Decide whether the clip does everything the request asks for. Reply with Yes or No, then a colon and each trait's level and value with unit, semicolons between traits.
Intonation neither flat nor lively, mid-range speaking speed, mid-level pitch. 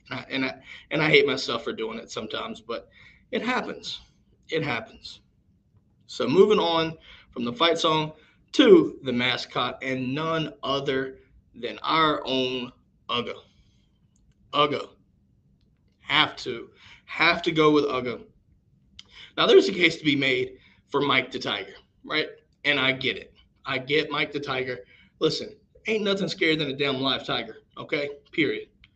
Yes: average, 3.9 semitones; average, 155 wpm; medium, 145 Hz